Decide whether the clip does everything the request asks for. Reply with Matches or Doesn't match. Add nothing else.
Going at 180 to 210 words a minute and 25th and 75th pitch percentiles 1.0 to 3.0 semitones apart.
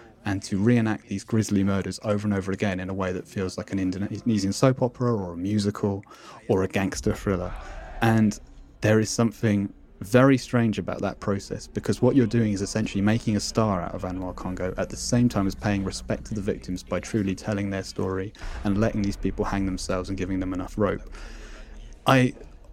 Matches